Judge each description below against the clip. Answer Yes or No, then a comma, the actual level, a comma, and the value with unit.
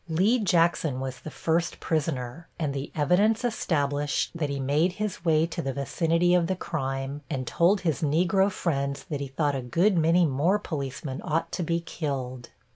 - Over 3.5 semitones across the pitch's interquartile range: Yes, average, 3.9 semitones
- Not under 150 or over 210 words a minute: Yes, average, 180 wpm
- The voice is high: No, medium, 160 Hz